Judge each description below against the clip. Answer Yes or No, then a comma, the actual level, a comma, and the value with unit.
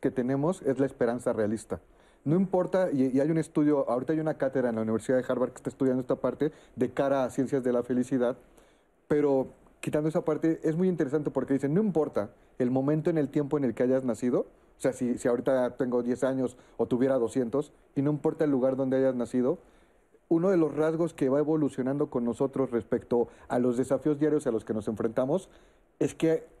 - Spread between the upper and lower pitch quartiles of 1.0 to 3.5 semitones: Yes, average, 3.2 semitones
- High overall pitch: No, low, 135 Hz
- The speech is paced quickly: Yes, fast, 215 wpm